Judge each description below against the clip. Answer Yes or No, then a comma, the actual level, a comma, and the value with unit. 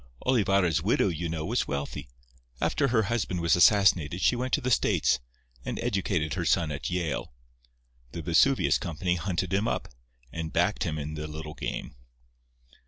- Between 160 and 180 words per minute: Yes, average, 165 wpm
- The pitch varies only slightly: No, average, 4.3 semitones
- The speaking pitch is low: Yes, very low, 85 Hz